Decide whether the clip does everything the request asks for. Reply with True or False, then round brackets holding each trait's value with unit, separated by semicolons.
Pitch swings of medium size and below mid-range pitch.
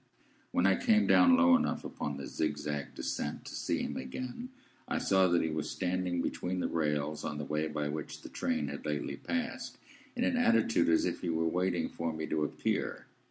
False (7.4 semitones; 85 Hz)